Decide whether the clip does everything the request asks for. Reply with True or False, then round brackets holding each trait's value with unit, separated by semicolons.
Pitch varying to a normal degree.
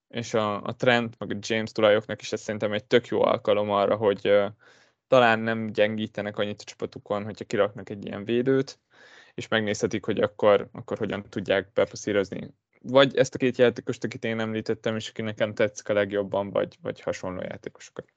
True (3.5 semitones)